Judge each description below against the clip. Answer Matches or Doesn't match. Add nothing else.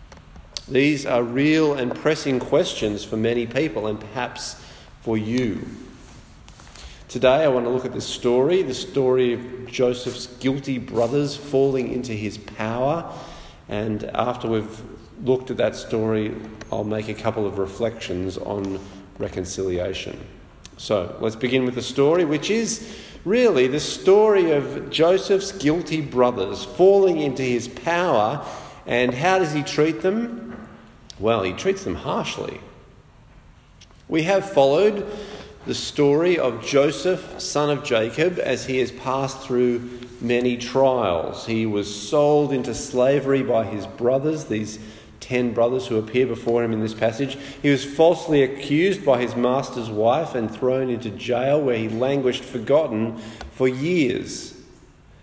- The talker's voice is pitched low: Matches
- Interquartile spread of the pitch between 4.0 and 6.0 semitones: Matches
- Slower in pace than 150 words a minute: Matches